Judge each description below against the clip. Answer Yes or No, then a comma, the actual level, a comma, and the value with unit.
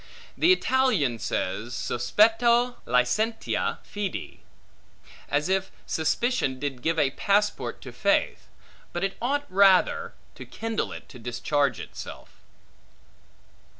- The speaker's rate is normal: No, slow, 110 wpm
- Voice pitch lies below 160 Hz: No, high, 190 Hz